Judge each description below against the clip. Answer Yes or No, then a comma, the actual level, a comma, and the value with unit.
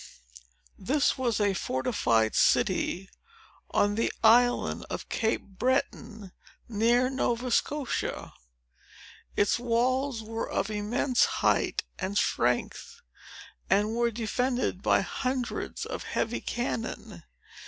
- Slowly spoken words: Yes, slow, 100 wpm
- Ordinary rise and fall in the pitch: Yes, average, 3.3 semitones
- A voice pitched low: No, high, 230 Hz